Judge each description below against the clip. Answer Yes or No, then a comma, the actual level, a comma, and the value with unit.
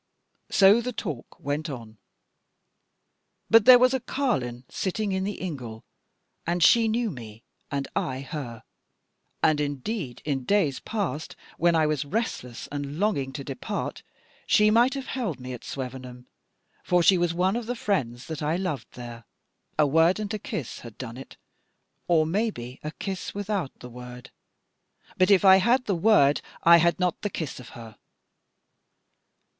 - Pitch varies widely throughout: Yes, wide, 7.7 semitones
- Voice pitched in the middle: Yes, medium, 160 Hz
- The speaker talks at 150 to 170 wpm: Yes, average, 160 wpm